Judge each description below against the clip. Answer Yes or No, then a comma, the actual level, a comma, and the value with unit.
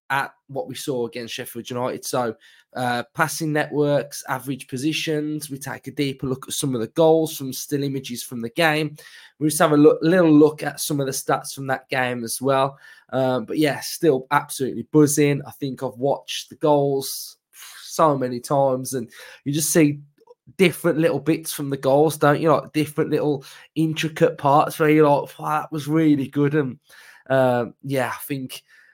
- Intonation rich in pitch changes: No, average, 2.7 semitones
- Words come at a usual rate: Yes, average, 190 wpm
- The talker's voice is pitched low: No, medium, 145 Hz